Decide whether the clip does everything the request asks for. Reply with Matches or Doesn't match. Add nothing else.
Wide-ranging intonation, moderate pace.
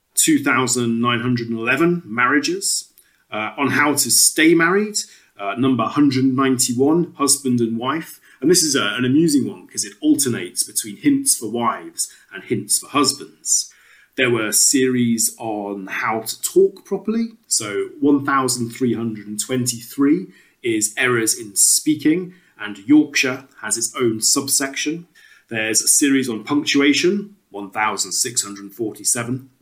Doesn't match